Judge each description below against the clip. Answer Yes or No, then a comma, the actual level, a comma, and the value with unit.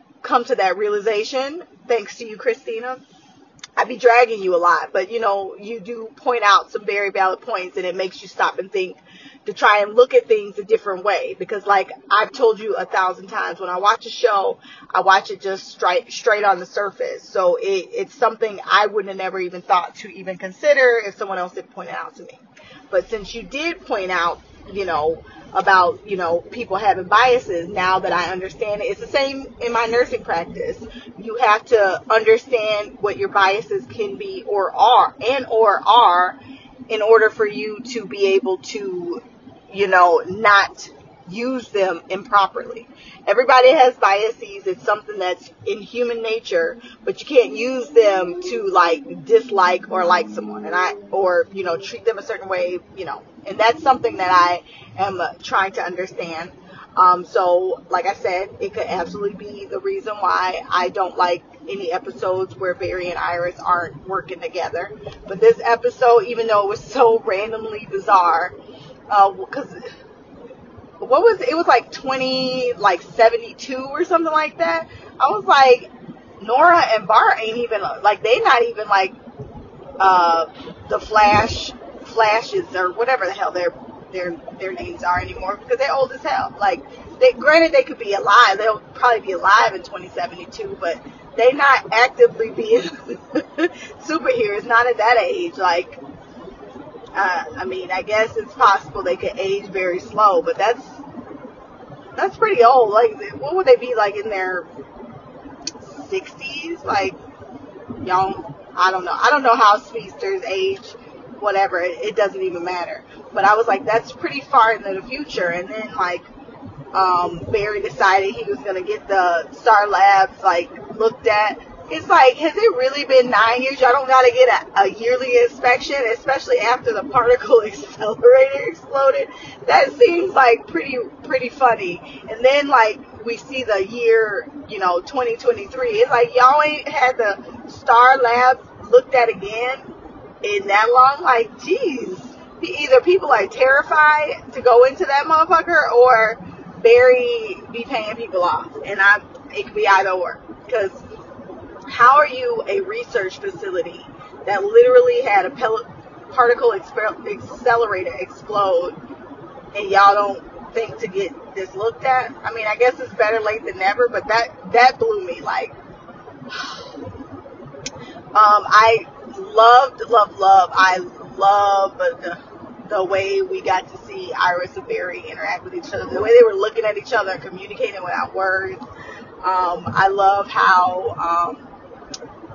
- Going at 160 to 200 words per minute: Yes, average, 170 wpm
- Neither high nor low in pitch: No, high, 235 Hz